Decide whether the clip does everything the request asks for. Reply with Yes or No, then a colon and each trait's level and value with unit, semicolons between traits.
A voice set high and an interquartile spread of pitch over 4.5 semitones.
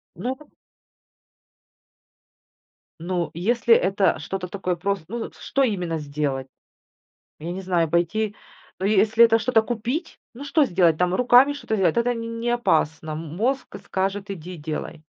Yes: high, 195 Hz; wide, 5.4 semitones